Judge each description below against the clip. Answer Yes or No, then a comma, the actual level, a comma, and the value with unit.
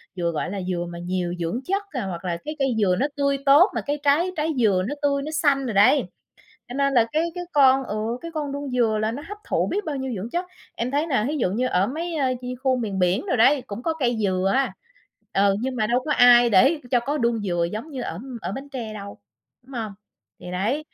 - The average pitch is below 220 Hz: No, very high, 250 Hz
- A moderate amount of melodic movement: No, wide, 6.0 semitones